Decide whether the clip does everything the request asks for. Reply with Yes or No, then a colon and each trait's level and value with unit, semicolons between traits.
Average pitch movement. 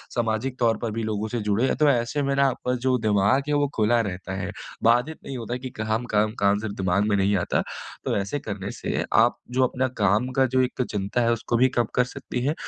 Yes: average, 3.7 semitones